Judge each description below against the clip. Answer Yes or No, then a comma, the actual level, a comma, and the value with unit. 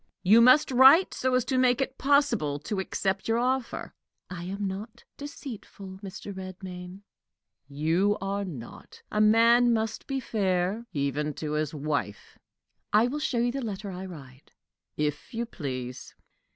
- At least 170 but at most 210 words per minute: No, average, 150 wpm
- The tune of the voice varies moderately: No, wide, 5.7 semitones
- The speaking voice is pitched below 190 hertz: No, high, 200 Hz